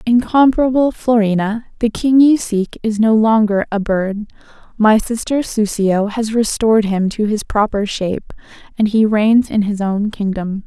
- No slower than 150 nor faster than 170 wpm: Yes, average, 160 wpm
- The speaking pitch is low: No, high, 215 Hz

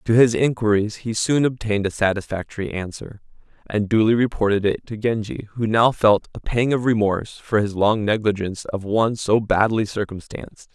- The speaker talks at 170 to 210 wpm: Yes, average, 175 wpm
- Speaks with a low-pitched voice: Yes, low, 110 Hz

